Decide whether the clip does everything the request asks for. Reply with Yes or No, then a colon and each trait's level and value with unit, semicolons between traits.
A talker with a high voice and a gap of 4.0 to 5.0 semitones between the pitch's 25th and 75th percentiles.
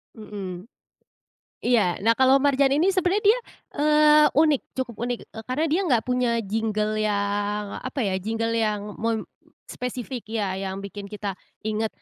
Yes: high, 225 Hz; average, 4.4 semitones